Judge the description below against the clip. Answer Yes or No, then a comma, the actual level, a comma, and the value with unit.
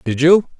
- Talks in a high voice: No, medium, 160 Hz